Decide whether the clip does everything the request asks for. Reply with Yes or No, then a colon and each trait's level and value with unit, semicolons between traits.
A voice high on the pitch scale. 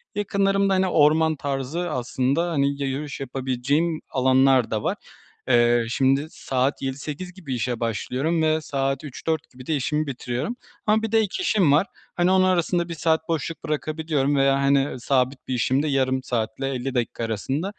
No: medium, 140 Hz